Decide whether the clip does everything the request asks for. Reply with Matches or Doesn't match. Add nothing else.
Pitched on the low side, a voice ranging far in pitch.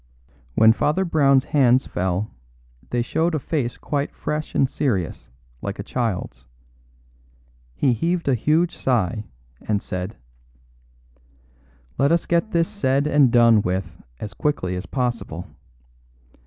Matches